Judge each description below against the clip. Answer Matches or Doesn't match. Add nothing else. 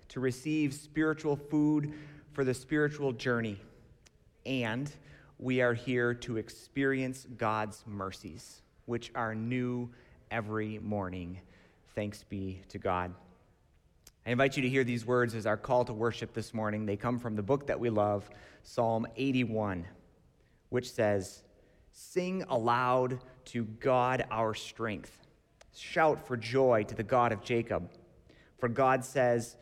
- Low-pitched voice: Matches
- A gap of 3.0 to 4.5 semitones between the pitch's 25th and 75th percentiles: Matches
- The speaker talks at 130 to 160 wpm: Matches